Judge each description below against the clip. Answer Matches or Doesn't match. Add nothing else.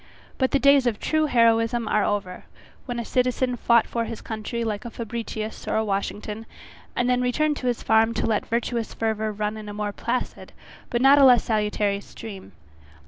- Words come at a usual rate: Matches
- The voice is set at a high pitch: Matches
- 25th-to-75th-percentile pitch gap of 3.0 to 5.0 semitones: Doesn't match